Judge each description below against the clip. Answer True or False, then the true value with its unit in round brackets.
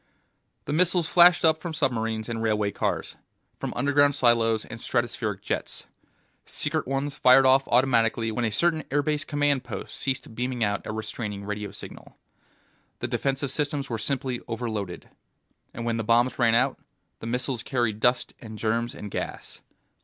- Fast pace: False (160 wpm)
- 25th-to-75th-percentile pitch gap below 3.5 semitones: False (3.8 semitones)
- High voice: False (120 Hz)